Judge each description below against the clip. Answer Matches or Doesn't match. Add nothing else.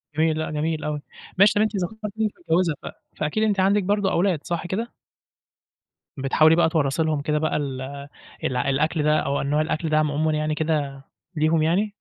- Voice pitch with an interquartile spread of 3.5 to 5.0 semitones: Matches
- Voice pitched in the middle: Matches